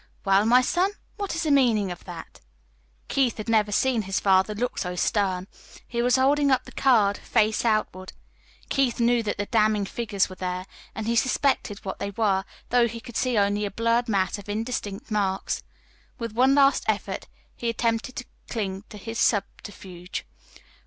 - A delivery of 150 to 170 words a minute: No, average, 180 wpm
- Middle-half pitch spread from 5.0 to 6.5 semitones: No, average, 3.4 semitones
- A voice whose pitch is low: No, high, 220 Hz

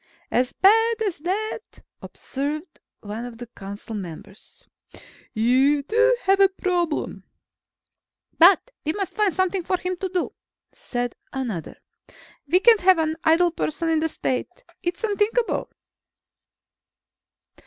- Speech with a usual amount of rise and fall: No, wide, 6.8 semitones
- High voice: Yes, very high, 345 Hz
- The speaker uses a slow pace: Yes, slow, 125 wpm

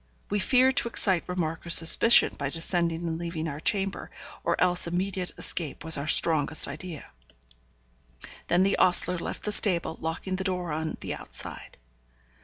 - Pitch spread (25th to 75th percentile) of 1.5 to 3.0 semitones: Yes, narrow, 2.6 semitones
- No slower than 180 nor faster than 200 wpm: No, average, 160 wpm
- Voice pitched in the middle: Yes, medium, 170 Hz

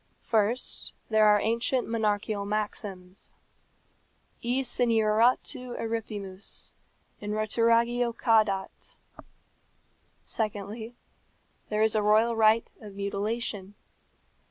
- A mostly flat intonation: Yes, narrow, 2.0 semitones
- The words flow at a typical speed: No, slow, 85 wpm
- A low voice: No, high, 215 Hz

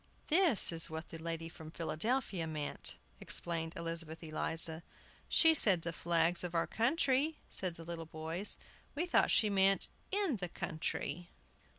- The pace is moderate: Yes, average, 150 wpm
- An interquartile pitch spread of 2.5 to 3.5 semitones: No, average, 4.8 semitones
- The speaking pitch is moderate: Yes, medium, 170 Hz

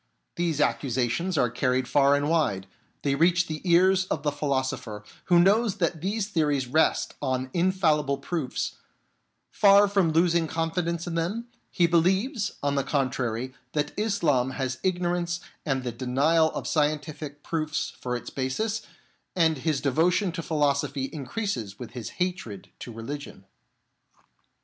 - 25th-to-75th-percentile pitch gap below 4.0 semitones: No, average, 4.8 semitones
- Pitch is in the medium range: Yes, medium, 155 Hz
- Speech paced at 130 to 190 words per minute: Yes, average, 140 wpm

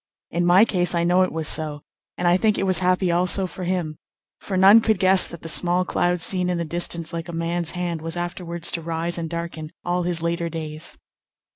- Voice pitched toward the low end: No, medium, 175 Hz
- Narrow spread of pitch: Yes, narrow, 1.5 semitones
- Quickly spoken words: Yes, fast, 225 wpm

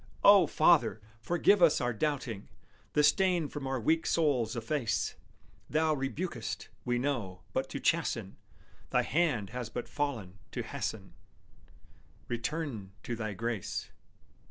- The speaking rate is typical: No, slow, 130 wpm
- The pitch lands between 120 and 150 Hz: Yes, low, 135 Hz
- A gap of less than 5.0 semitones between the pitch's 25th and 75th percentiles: No, wide, 5.4 semitones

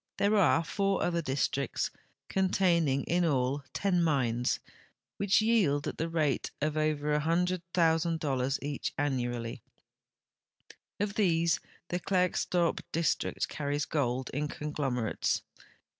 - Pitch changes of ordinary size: Yes, average, 4.1 semitones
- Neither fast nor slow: No, slow, 115 wpm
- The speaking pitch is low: No, medium, 155 Hz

